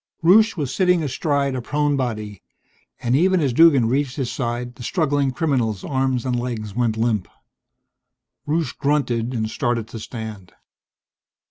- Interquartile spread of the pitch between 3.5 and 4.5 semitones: Yes, average, 4.0 semitones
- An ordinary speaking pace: Yes, average, 145 wpm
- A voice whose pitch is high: No, low, 125 Hz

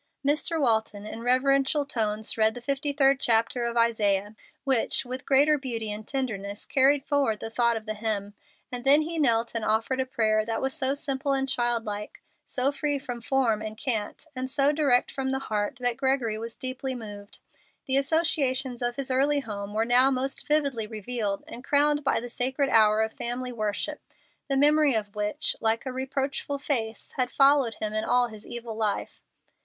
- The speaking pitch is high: Yes, high, 245 Hz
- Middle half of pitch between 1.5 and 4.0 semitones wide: Yes, average, 3.7 semitones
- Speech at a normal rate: Yes, average, 190 wpm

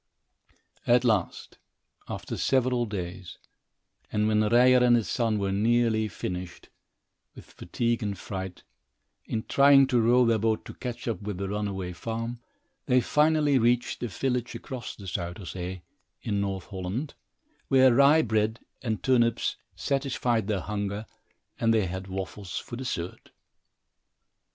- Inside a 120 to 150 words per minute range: Yes, average, 140 wpm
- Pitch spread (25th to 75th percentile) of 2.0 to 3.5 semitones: No, average, 3.9 semitones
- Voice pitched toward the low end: Yes, low, 110 Hz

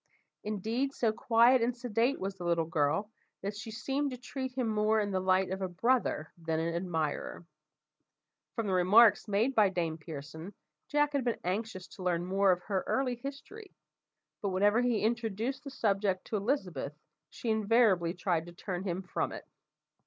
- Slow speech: No, average, 175 wpm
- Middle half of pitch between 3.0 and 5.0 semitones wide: Yes, average, 4.7 semitones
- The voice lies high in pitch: Yes, high, 205 Hz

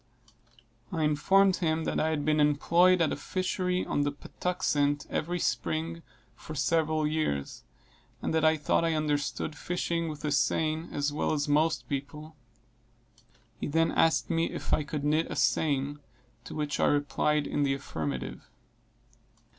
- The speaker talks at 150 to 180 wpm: Yes, average, 155 wpm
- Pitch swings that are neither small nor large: No, narrow, 2.1 semitones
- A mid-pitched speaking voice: Yes, medium, 155 Hz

